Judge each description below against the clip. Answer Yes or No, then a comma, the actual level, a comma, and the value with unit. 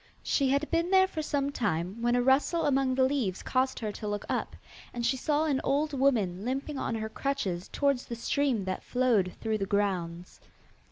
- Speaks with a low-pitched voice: No, very high, 255 Hz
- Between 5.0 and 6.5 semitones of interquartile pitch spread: Yes, average, 5.3 semitones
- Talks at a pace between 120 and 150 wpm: No, average, 200 wpm